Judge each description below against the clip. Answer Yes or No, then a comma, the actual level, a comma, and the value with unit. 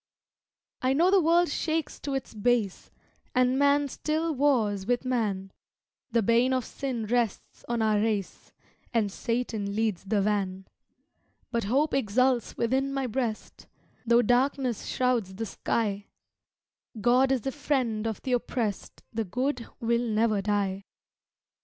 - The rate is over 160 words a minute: No, average, 140 wpm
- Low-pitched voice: No, high, 235 Hz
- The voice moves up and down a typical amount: Yes, average, 3.9 semitones